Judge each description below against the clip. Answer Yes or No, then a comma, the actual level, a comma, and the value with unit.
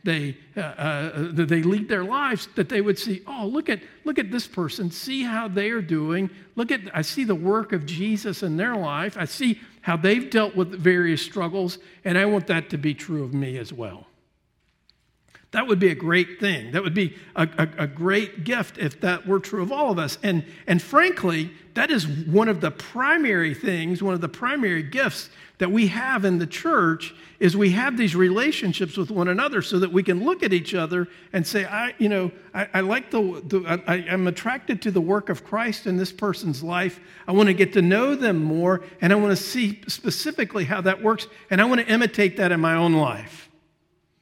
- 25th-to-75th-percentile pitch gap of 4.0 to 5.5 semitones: No, average, 3.5 semitones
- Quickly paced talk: Yes, fast, 215 wpm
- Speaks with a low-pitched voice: No, high, 190 Hz